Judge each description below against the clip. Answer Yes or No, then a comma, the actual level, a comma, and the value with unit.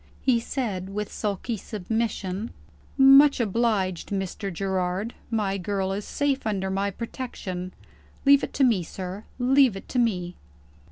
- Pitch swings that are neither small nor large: Yes, average, 3.9 semitones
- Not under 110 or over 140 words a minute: Yes, slow, 135 wpm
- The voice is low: No, high, 205 Hz